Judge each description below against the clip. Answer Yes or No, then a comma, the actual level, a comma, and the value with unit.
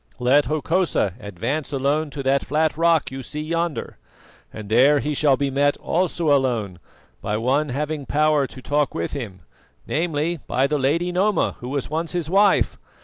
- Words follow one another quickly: No, average, 170 wpm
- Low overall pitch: No, medium, 145 Hz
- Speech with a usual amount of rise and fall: Yes, average, 3.0 semitones